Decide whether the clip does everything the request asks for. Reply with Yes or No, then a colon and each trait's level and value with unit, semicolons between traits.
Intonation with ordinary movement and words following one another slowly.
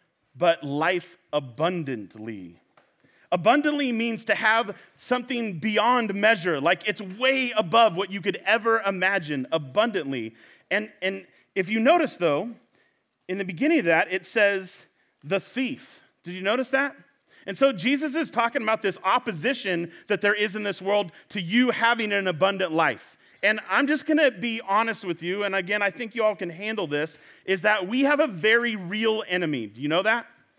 No: average, 4.4 semitones; average, 175 wpm